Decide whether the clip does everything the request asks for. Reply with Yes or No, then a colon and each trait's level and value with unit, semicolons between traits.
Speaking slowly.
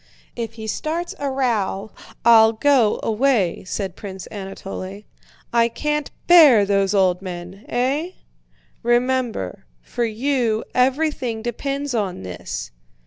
Yes: slow, 115 wpm